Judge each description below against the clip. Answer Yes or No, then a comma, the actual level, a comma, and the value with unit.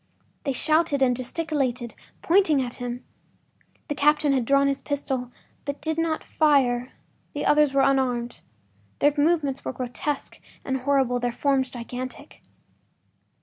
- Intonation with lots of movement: No, average, 2.9 semitones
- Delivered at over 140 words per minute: No, slow, 135 wpm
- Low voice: No, very high, 275 Hz